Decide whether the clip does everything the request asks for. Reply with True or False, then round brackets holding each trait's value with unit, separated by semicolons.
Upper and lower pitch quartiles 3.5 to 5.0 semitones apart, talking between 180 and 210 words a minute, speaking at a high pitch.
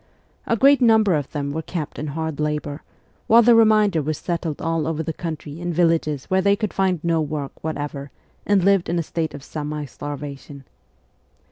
False (4.1 semitones; 190 wpm; 160 Hz)